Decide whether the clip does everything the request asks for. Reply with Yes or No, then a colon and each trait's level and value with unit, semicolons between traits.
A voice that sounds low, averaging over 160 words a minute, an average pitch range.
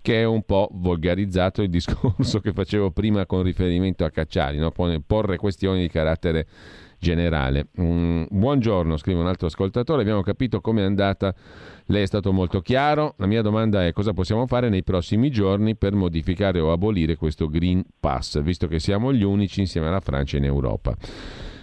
Yes: very low, 95 Hz; fast, 170 wpm; average, 3.5 semitones